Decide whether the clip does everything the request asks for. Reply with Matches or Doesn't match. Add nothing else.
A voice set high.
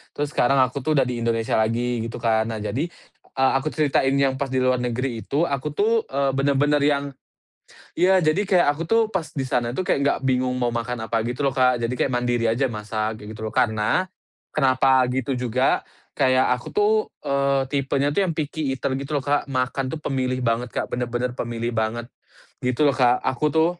Doesn't match